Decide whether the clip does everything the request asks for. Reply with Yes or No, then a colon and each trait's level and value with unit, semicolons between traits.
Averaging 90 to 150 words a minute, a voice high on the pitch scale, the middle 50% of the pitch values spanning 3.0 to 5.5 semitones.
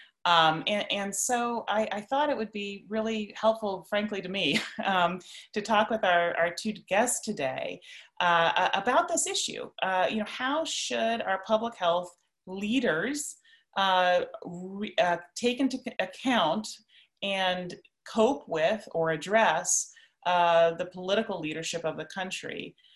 Yes: average, 145 wpm; high, 205 Hz; average, 4.1 semitones